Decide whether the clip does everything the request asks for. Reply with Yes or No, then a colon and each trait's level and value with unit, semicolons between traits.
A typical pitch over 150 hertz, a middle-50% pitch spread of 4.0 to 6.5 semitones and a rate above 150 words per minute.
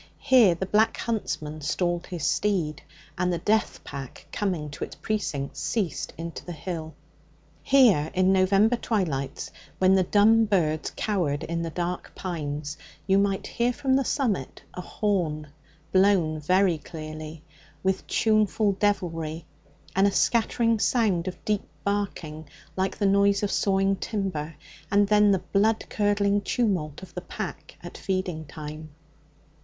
No: medium, 185 Hz; average, 4.5 semitones; average, 145 wpm